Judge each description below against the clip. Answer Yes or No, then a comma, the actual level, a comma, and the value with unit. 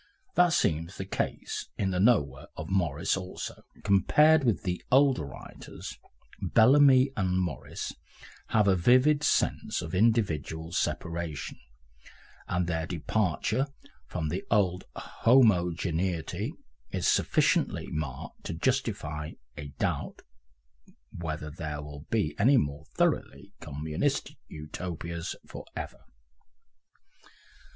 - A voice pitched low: Yes, very low, 90 Hz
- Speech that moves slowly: Yes, slow, 110 wpm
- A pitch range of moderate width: No, wide, 5.7 semitones